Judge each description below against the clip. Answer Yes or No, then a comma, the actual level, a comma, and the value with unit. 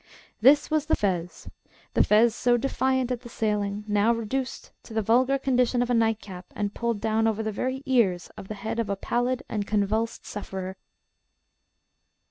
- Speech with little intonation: No, average, 3.2 semitones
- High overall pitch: Yes, high, 225 Hz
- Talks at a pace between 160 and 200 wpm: Yes, average, 175 wpm